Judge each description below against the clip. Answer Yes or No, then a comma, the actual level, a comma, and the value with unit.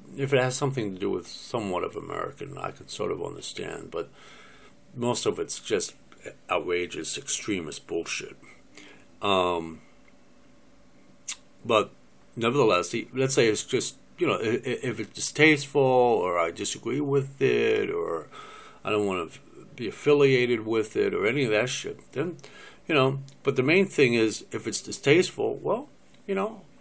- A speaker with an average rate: Yes, average, 150 wpm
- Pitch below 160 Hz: Yes, low, 135 Hz